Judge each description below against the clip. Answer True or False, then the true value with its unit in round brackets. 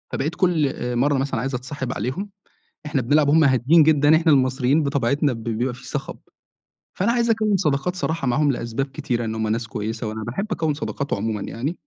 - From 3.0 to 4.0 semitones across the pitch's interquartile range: False (4.6 semitones)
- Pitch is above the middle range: False (140 Hz)